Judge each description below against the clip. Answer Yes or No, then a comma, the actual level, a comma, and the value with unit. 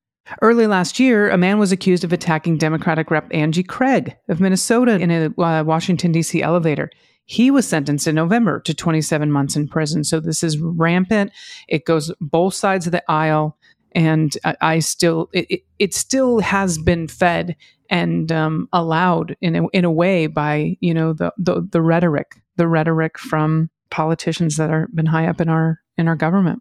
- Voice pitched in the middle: Yes, medium, 165 Hz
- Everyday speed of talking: Yes, average, 185 wpm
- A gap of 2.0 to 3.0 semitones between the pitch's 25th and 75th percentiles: Yes, narrow, 2.4 semitones